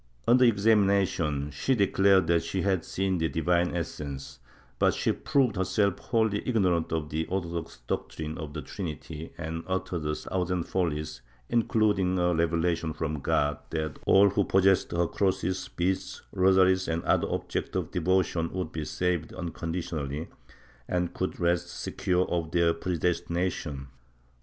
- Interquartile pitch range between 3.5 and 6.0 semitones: No, average, 2.8 semitones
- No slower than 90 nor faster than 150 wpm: Yes, average, 140 wpm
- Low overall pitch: Yes, very low, 85 Hz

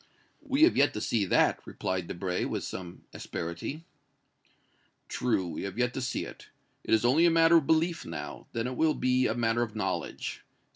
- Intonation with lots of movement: Yes, wide, 8.4 semitones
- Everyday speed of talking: Yes, average, 190 wpm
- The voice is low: Yes, low, 120 Hz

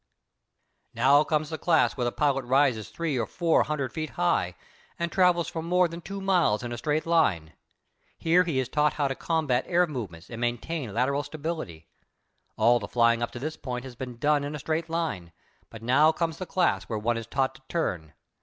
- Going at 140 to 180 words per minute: No, fast, 205 wpm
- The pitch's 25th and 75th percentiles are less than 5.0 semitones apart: No, wide, 5.4 semitones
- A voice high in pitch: No, medium, 145 Hz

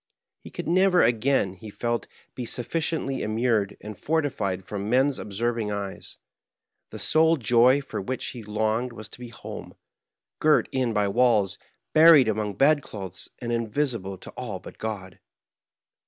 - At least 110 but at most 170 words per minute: Yes, average, 145 wpm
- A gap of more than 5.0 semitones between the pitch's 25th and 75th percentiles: No, average, 4.1 semitones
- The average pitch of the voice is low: Yes, low, 115 Hz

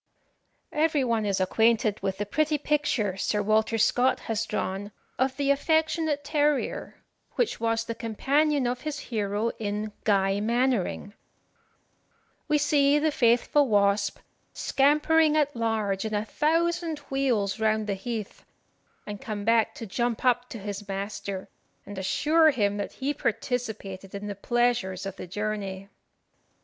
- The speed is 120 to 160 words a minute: Yes, average, 140 wpm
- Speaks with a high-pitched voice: Yes, high, 225 Hz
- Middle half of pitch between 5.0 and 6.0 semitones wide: Yes, wide, 5.6 semitones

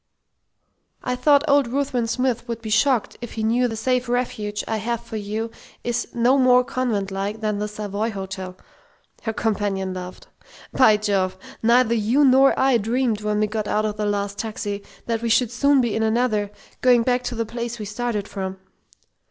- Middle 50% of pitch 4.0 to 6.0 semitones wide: No, average, 2.9 semitones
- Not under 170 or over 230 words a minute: Yes, average, 185 wpm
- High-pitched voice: Yes, high, 225 Hz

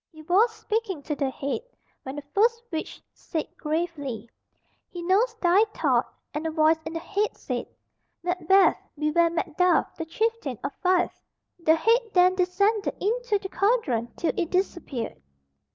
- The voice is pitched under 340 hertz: No, very high, 350 Hz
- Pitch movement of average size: Yes, average, 4.4 semitones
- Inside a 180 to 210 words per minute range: No, average, 150 wpm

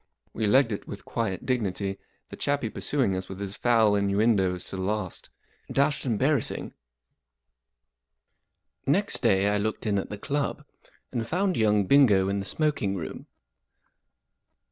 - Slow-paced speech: No, average, 145 wpm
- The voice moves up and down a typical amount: Yes, average, 4.6 semitones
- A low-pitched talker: Yes, low, 105 Hz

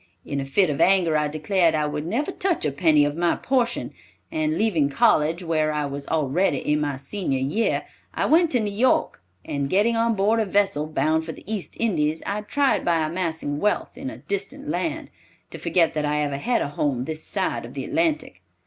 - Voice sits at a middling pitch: Yes, medium, 165 Hz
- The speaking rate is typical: No, fast, 210 wpm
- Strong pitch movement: Yes, wide, 6.7 semitones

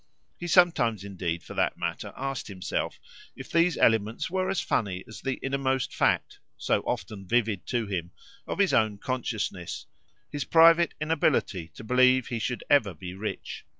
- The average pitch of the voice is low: Yes, low, 120 Hz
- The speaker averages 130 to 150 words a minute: No, average, 160 wpm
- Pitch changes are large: Yes, wide, 6.3 semitones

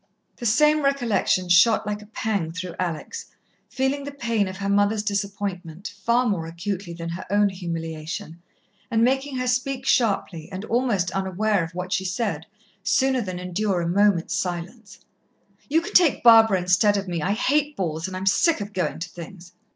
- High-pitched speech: Yes, high, 200 Hz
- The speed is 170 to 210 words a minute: Yes, average, 175 wpm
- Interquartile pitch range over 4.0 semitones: Yes, average, 4.7 semitones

